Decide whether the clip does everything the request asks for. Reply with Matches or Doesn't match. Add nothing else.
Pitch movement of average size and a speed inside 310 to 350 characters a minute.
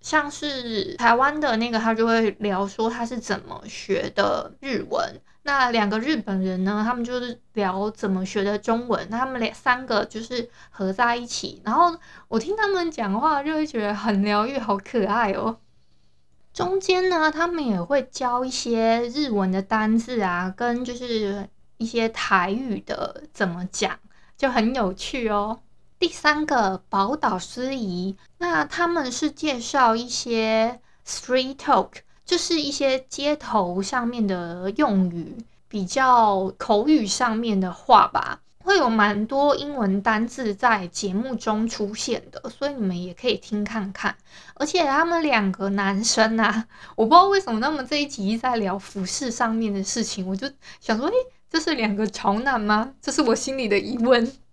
Doesn't match